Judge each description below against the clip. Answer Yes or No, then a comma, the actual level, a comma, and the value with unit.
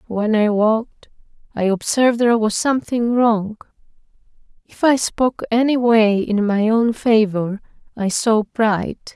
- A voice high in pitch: Yes, high, 220 Hz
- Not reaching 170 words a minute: Yes, average, 140 wpm